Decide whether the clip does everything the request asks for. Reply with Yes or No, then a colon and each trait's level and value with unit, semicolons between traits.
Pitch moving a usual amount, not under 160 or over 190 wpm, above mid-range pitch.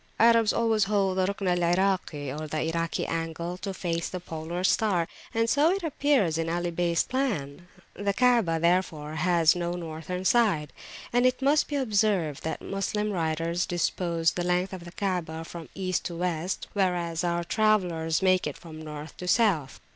No: average, 3.5 semitones; average, 170 wpm; medium, 180 Hz